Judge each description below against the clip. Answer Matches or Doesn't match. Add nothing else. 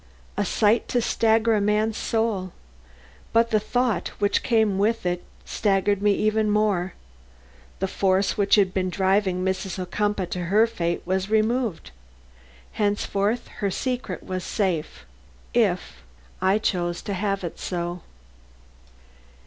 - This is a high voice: Matches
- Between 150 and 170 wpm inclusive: Doesn't match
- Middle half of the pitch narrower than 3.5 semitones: Matches